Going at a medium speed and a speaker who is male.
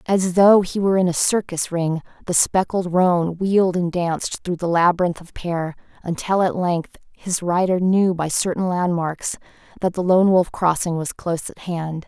No: average, 185 wpm; female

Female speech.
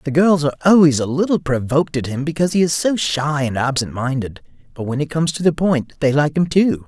No: male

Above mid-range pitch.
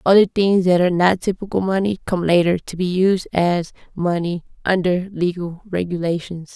No: medium, 180 Hz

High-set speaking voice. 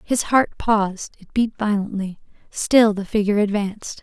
Yes: high, 210 Hz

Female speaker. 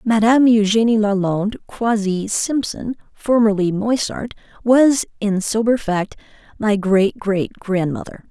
Yes: female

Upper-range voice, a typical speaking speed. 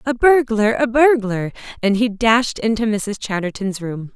Yes: high, 220 Hz; average, 145 wpm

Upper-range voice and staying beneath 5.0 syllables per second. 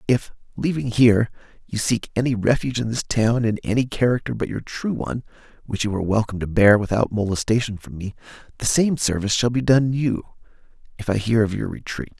No: low, 115 Hz; 4.6 syllables/s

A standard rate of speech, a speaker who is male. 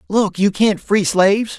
Yes: average, 190 wpm; male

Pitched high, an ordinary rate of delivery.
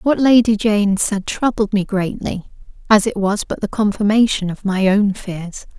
Yes: high, 205 Hz; average, 175 wpm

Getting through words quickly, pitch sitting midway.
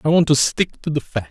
Yes: fast, 320 wpm; medium, 145 Hz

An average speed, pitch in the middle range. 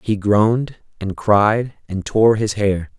No: average, 160 wpm; low, 105 Hz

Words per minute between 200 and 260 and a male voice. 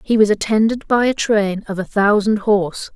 No: fast, 205 wpm; female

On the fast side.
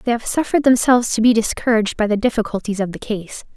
Yes: fast, 220 wpm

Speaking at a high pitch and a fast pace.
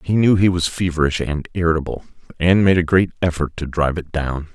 No: very low, 85 Hz; fast, 210 wpm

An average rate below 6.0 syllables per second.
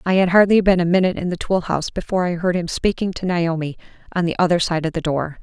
No: 6.7 syllables/s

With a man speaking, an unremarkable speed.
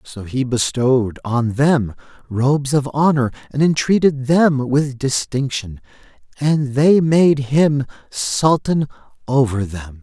No: male; slow, 120 wpm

